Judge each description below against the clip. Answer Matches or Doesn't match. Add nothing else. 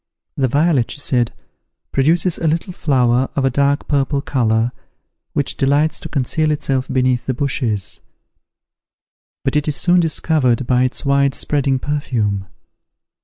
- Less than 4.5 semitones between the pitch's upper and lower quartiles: Matches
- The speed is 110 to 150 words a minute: Matches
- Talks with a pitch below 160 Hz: Matches